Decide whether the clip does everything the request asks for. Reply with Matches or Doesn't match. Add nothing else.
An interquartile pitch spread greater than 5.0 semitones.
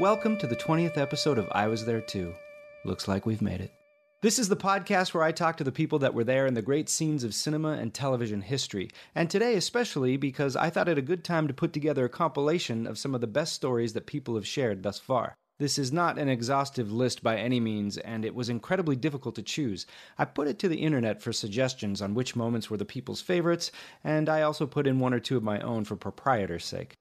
Matches